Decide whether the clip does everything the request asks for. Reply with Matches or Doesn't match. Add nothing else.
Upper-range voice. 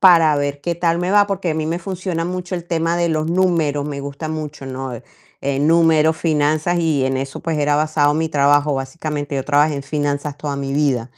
Doesn't match